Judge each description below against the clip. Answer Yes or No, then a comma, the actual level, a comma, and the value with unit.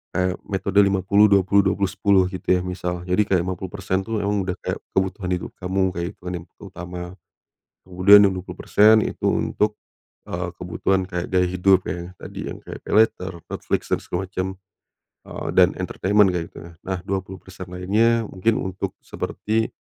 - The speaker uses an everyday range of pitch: No, narrow, 1.7 semitones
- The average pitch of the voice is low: Yes, very low, 95 Hz